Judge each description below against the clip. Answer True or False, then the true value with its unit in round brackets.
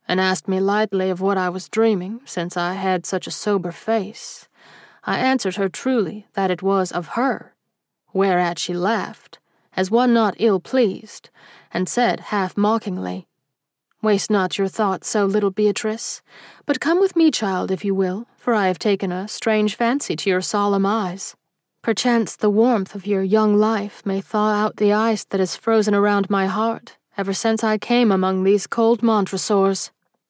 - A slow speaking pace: False (175 wpm)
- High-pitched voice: True (205 Hz)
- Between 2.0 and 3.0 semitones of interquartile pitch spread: True (2.7 semitones)